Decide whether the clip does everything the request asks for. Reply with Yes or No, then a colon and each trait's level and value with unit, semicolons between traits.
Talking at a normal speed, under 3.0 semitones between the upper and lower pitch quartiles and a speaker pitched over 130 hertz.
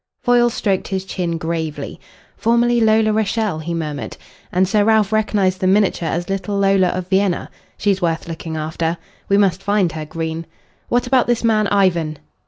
No: average, 170 wpm; average, 4.3 semitones; high, 190 Hz